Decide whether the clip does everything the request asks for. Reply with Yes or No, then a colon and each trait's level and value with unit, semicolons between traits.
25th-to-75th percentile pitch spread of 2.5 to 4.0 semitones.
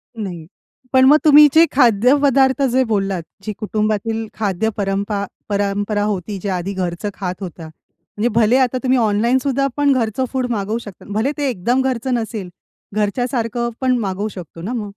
No: average, 4.4 semitones